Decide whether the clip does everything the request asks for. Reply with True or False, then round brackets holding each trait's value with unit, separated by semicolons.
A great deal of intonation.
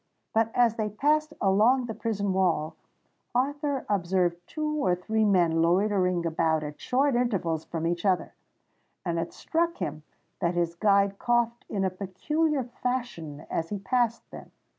True (6.0 semitones)